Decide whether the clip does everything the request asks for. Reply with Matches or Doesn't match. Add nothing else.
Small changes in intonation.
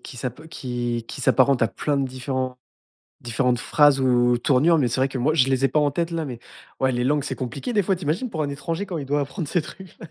Doesn't match